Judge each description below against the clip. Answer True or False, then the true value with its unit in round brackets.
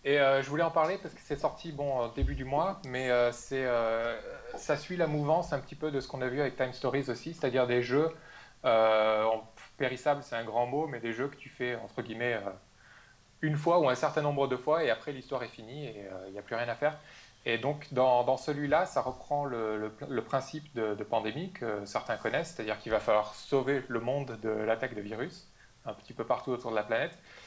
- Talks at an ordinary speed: False (240 wpm)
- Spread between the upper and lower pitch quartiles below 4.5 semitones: True (4.1 semitones)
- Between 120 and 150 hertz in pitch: True (130 Hz)